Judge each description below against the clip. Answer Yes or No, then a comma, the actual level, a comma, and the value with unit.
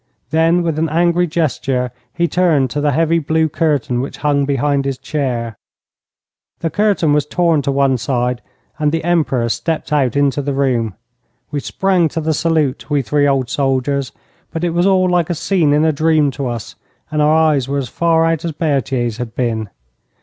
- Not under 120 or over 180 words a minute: No, average, 190 wpm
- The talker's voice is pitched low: No, medium, 150 Hz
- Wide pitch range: No, average, 3.4 semitones